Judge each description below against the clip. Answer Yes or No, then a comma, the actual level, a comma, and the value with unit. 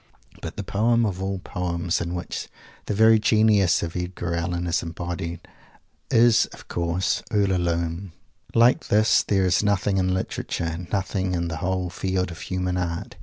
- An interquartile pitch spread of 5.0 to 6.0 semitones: No, narrow, 2.5 semitones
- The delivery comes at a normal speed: Yes, average, 155 wpm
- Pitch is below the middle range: Yes, very low, 90 Hz